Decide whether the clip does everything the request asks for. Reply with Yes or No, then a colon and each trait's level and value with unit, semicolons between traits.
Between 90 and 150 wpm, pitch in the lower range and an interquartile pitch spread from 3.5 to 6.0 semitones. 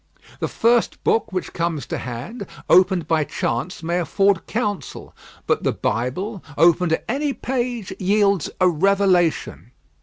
No: average, 140 wpm; medium, 185 Hz; average, 4.3 semitones